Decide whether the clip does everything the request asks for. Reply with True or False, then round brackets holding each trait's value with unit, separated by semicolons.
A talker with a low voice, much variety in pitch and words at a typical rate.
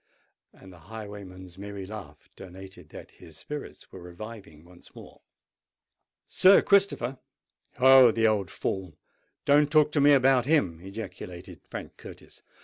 False (100 Hz; 6.4 semitones; 130 wpm)